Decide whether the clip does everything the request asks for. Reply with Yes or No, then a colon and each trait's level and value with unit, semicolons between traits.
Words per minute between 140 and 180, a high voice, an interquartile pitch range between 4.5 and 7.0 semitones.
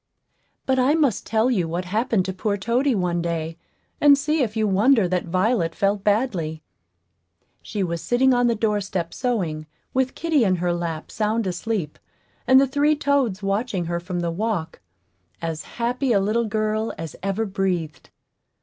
Yes: average, 170 wpm; high, 205 Hz; wide, 5.6 semitones